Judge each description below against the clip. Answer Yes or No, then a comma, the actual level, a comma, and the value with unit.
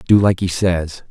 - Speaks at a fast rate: Yes, fast, 215 wpm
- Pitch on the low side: Yes, very low, 90 Hz